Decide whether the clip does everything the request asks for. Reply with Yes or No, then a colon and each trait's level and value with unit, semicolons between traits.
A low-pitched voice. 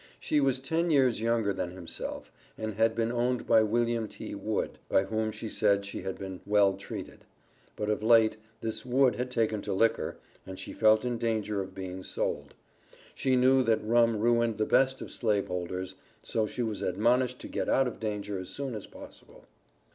Yes: low, 110 Hz